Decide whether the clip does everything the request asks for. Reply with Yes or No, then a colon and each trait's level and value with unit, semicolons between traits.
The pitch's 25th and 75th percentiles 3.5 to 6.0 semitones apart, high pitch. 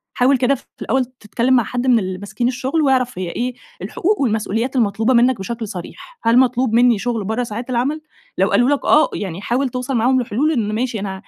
No: average, 2.8 semitones; high, 245 Hz